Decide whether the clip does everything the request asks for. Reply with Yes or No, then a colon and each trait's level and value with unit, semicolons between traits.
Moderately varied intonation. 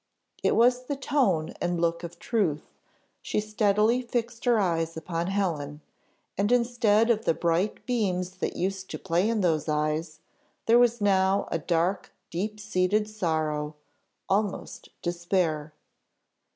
Yes: average, 4.5 semitones